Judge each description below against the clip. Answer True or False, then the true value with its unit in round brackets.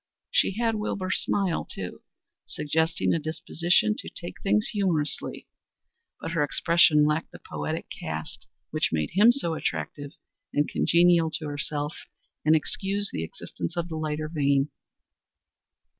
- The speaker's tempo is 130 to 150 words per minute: True (135 wpm)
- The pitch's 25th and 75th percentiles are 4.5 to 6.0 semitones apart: False (3.3 semitones)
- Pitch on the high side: False (160 Hz)